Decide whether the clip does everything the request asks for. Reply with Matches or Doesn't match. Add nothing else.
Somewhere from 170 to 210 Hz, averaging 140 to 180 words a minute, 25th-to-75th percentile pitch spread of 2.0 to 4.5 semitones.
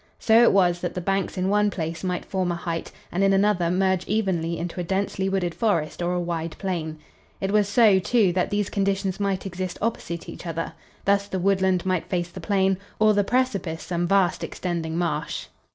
Doesn't match